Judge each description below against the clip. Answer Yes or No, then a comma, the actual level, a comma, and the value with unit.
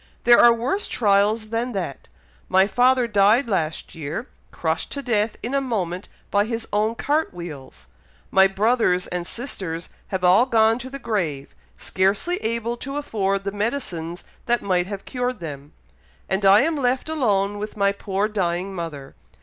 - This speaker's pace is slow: No, average, 165 wpm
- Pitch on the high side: Yes, high, 205 Hz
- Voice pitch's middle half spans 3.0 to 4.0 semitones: No, average, 4.6 semitones